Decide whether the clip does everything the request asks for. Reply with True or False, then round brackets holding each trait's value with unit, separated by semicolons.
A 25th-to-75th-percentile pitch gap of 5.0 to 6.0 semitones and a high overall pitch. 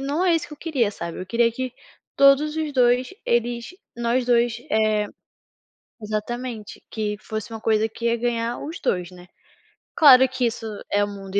False (3.1 semitones; 235 Hz)